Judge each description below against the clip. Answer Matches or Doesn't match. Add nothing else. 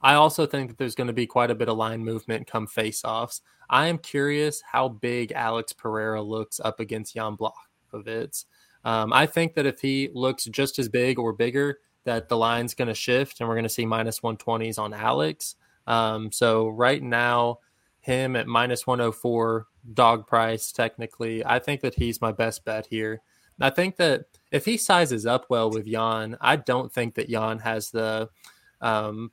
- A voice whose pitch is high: Doesn't match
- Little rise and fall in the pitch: Matches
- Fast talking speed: Doesn't match